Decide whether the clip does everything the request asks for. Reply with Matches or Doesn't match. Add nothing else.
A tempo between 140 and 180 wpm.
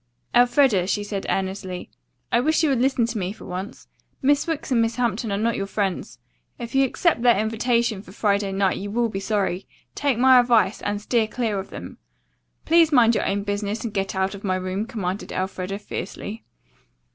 Doesn't match